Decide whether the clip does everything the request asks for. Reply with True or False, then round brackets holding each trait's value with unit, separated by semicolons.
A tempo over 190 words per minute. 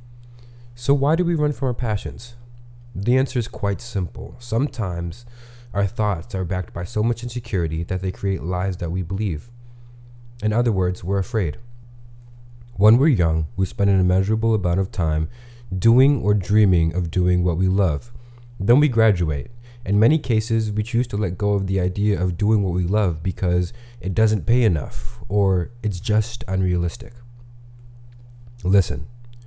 False (165 wpm)